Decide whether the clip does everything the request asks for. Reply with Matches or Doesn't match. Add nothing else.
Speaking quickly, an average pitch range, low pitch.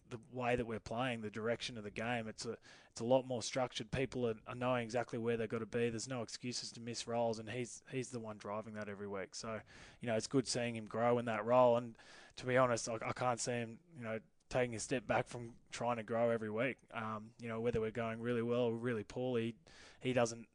Doesn't match